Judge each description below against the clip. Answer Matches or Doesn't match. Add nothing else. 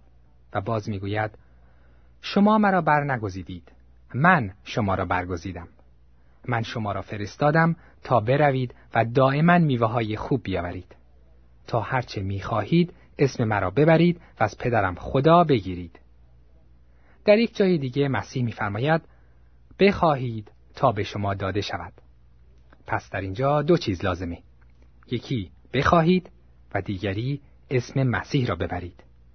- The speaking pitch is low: Matches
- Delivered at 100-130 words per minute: Matches